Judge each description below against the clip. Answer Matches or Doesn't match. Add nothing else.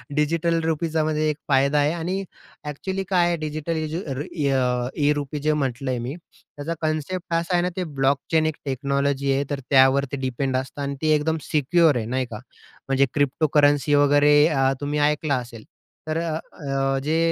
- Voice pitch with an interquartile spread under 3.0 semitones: Matches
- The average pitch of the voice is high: Doesn't match